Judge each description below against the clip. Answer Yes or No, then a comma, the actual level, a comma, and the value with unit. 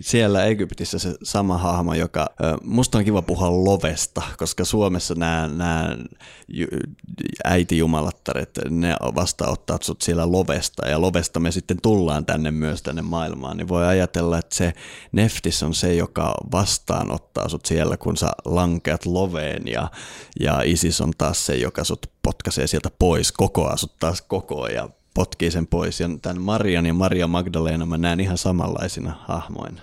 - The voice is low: Yes, very low, 85 Hz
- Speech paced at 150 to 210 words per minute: Yes, fast, 155 wpm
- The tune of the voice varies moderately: No, narrow, 2.0 semitones